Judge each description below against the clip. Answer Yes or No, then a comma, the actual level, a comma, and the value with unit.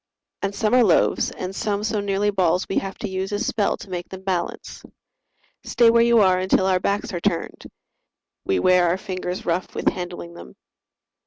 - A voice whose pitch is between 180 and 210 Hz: Yes, high, 190 Hz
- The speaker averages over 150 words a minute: Yes, average, 190 wpm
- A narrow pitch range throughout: Yes, narrow, 2.1 semitones